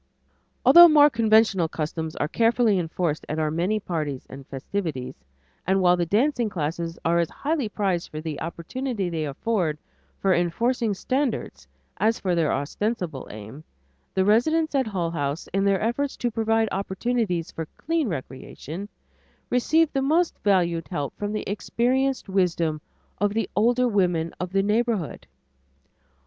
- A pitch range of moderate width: No, wide, 5.9 semitones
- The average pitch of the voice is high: Yes, high, 195 Hz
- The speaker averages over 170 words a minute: No, average, 150 wpm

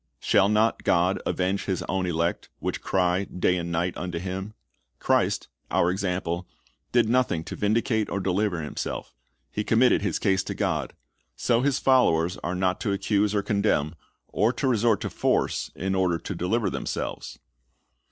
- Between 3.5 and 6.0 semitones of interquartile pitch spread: No, average, 3.1 semitones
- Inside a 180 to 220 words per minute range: No, average, 160 wpm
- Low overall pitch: Yes, very low, 95 Hz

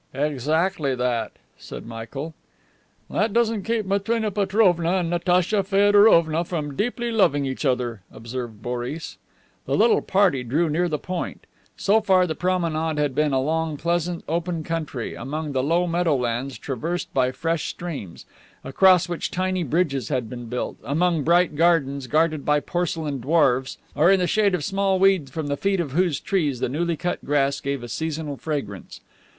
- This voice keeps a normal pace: Yes, average, 160 wpm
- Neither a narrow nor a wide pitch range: Yes, average, 4.7 semitones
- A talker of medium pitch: Yes, medium, 160 Hz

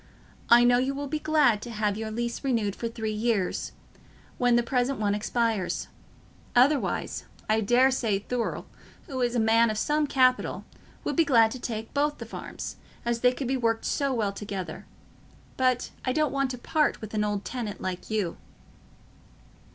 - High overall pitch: Yes, high, 235 Hz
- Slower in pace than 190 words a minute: Yes, average, 175 wpm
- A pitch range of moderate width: Yes, average, 3.2 semitones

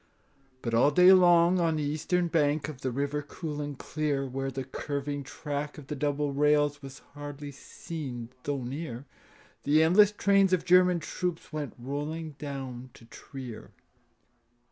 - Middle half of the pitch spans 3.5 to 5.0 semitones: No, average, 2.9 semitones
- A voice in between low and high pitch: Yes, medium, 145 Hz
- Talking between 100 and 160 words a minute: Yes, average, 155 wpm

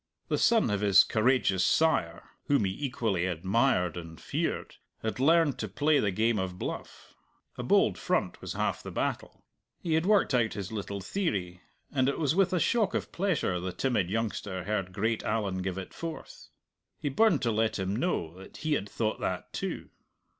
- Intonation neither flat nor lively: No, wide, 7.5 semitones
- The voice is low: Yes, low, 110 Hz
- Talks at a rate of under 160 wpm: No, average, 185 wpm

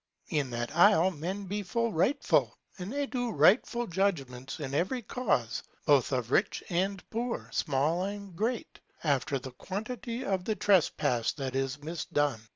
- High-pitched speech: No, medium, 175 Hz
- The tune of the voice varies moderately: No, wide, 6.9 semitones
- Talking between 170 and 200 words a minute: No, average, 160 wpm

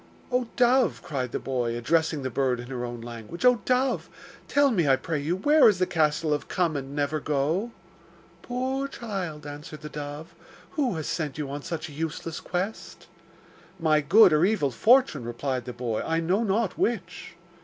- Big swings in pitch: Yes, wide, 6.7 semitones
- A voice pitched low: No, medium, 160 Hz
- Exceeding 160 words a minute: Yes, average, 185 wpm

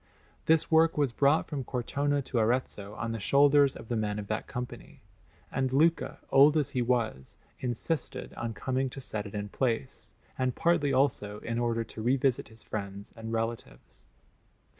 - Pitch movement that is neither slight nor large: Yes, average, 3.8 semitones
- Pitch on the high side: No, low, 125 Hz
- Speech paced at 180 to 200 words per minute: No, average, 170 wpm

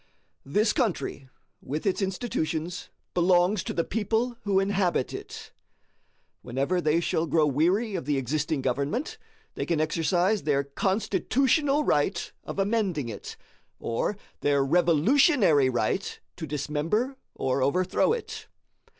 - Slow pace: Yes, slow, 125 wpm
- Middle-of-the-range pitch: Yes, medium, 175 Hz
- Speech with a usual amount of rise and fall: No, wide, 5.7 semitones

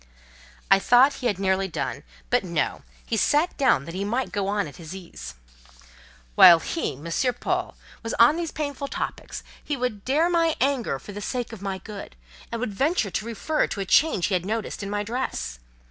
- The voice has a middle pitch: No, high, 210 Hz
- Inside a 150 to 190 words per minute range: No, average, 200 wpm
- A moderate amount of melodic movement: No, wide, 5.8 semitones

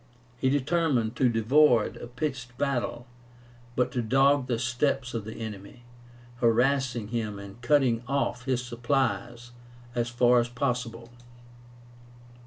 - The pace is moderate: No, slow, 125 wpm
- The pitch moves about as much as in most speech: No, narrow, 2.3 semitones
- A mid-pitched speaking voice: No, low, 120 Hz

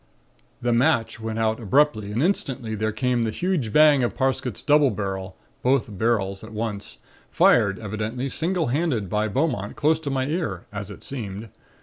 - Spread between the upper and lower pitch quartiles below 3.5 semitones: No, average, 4.7 semitones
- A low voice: Yes, low, 115 Hz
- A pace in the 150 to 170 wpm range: Yes, average, 165 wpm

